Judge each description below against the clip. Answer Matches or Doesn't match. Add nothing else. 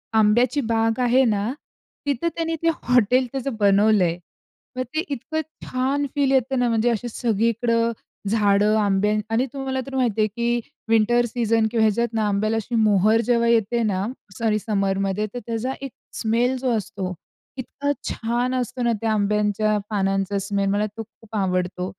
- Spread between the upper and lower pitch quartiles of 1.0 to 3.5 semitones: Matches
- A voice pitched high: Matches